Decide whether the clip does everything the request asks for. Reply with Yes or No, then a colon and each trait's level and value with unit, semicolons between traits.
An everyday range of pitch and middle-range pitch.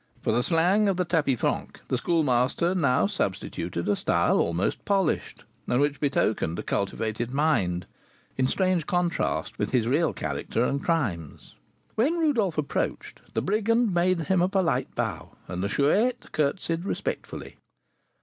No: wide, 7.4 semitones; medium, 160 Hz